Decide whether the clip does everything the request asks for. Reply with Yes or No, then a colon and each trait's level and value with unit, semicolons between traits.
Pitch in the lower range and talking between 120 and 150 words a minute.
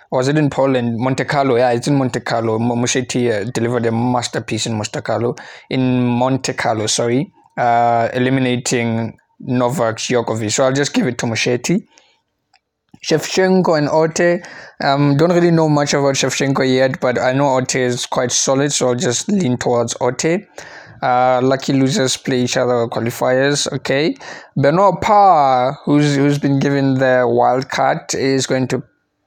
No: low, 130 Hz; average, 165 wpm